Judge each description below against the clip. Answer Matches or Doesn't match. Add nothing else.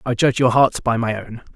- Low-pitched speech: Matches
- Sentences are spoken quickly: Matches